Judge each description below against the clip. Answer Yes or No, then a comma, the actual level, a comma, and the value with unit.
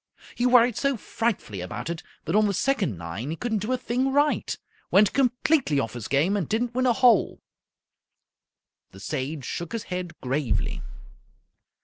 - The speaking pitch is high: Yes, high, 200 Hz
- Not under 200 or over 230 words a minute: No, average, 165 wpm